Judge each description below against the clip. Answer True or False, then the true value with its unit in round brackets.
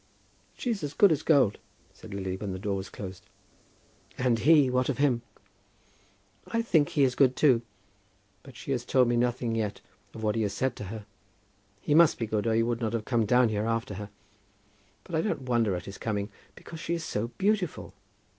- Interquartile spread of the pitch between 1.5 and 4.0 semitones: False (5.0 semitones)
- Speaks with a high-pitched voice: False (120 Hz)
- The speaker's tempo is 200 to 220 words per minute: True (205 wpm)